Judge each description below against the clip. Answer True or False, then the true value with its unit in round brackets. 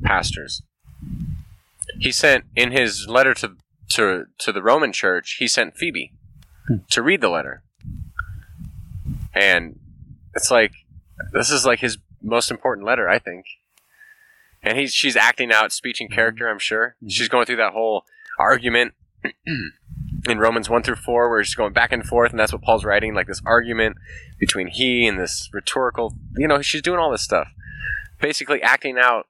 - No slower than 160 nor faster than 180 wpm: True (165 wpm)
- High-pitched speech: False (120 Hz)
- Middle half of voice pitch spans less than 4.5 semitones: False (5.0 semitones)